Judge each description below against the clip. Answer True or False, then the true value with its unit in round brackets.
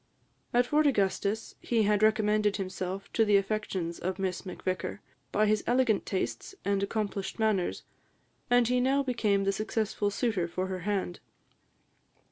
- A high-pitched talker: True (205 Hz)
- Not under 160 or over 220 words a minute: False (145 wpm)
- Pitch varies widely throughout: False (2.4 semitones)